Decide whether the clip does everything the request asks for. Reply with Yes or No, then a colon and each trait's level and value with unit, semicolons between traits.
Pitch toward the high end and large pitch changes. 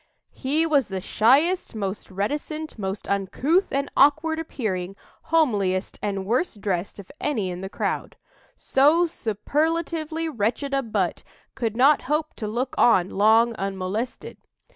Yes: high, 235 Hz; wide, 7.3 semitones